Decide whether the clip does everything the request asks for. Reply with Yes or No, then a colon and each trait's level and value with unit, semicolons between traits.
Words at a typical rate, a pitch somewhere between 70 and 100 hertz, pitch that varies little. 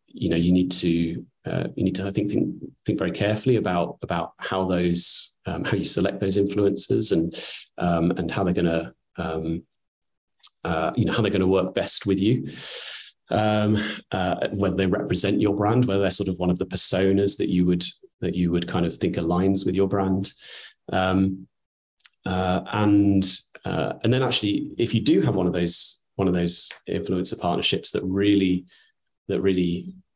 Yes: average, 185 wpm; very low, 95 Hz; narrow, 2.3 semitones